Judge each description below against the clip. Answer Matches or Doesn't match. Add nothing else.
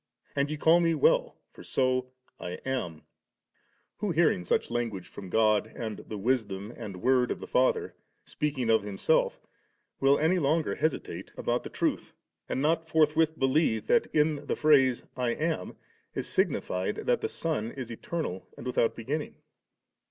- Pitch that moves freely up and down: Matches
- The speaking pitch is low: Matches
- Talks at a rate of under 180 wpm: Matches